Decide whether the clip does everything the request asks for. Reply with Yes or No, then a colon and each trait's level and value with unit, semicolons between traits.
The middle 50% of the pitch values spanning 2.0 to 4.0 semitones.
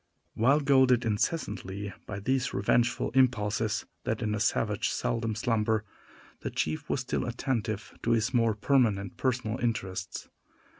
Yes: average, 3.3 semitones